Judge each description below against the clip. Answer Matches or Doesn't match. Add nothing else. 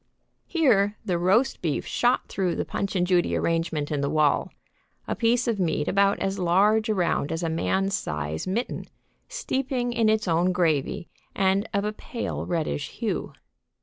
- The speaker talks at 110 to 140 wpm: Doesn't match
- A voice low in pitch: Doesn't match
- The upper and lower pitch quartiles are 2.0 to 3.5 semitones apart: Doesn't match